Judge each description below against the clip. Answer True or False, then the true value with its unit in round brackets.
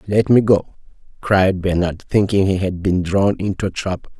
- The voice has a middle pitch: False (95 Hz)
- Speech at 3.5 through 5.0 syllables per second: True (4.7 syllables/s)